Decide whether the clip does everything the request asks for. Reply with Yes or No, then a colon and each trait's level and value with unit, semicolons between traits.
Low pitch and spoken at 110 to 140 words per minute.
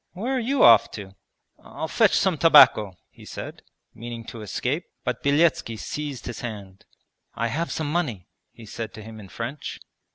No: low, 120 Hz; average, 170 wpm